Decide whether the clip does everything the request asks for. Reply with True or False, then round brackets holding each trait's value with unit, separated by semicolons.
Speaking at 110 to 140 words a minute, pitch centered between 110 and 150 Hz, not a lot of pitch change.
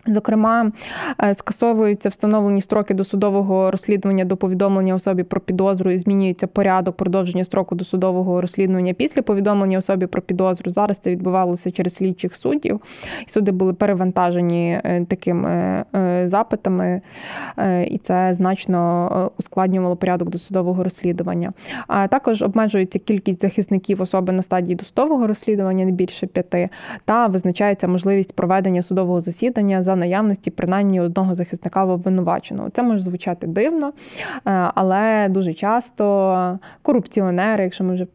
False (125 wpm; 190 Hz; 2.0 semitones)